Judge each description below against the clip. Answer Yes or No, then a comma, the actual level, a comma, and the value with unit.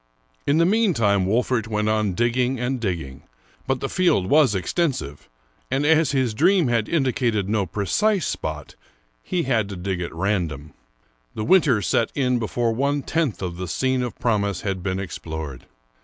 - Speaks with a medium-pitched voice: No, low, 115 Hz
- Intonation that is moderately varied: No, wide, 6.0 semitones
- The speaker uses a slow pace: No, average, 165 wpm